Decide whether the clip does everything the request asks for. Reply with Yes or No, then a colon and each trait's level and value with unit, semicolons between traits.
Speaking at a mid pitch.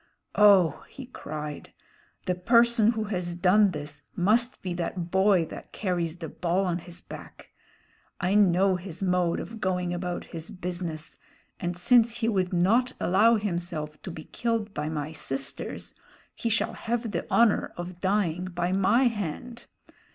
Yes: medium, 180 Hz